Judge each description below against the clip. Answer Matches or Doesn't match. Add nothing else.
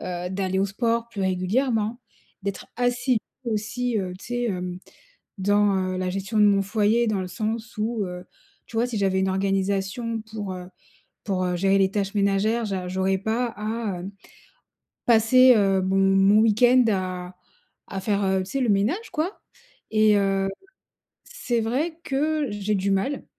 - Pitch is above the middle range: Matches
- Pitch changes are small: Doesn't match